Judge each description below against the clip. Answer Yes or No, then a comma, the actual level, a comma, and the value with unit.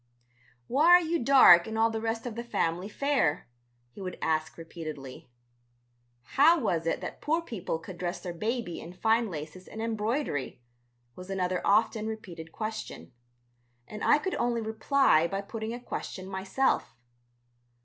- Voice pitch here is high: Yes, high, 215 Hz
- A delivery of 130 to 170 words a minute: Yes, average, 155 wpm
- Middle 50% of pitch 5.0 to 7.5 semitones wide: Yes, wide, 5.4 semitones